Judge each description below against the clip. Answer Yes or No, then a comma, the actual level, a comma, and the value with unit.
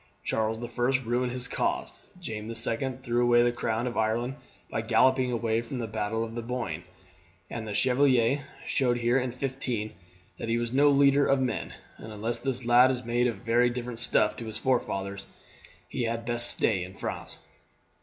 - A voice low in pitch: Yes, low, 120 Hz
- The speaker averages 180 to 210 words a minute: Yes, average, 185 wpm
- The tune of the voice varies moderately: No, narrow, 2.0 semitones